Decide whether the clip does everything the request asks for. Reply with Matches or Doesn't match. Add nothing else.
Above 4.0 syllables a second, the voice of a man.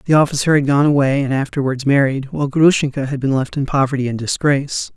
Matches